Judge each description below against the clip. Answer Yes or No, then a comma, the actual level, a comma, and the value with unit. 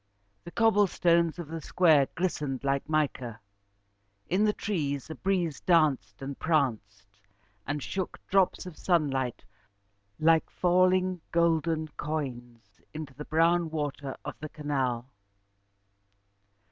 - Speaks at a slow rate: Yes, slow, 120 wpm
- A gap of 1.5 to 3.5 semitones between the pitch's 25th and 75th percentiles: No, average, 4.1 semitones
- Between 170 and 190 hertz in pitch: No, medium, 155 Hz